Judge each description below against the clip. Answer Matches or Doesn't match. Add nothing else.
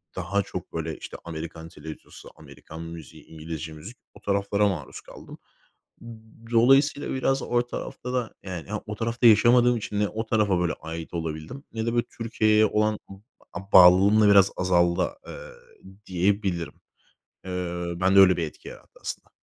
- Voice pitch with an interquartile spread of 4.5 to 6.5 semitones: Matches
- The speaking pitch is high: Doesn't match